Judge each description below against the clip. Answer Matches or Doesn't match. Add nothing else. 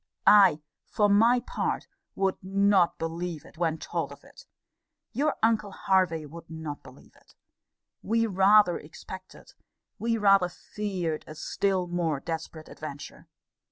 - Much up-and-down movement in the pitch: Doesn't match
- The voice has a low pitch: Doesn't match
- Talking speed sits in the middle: Doesn't match